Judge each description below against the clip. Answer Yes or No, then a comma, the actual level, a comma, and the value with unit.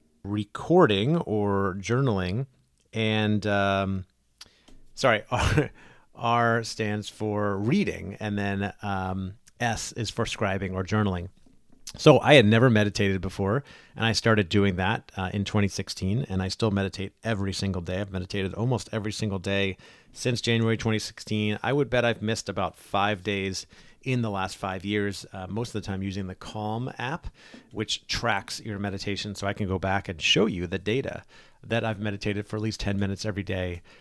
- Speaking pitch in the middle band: No, low, 105 Hz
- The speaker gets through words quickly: No, average, 170 wpm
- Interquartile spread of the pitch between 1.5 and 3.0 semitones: Yes, narrow, 2.4 semitones